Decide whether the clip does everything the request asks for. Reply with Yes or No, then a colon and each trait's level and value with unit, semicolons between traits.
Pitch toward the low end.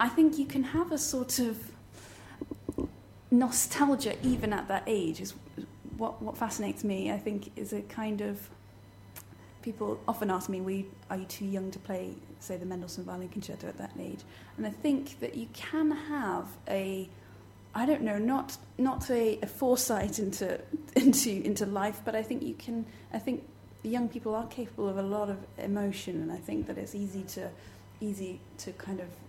No: high, 210 Hz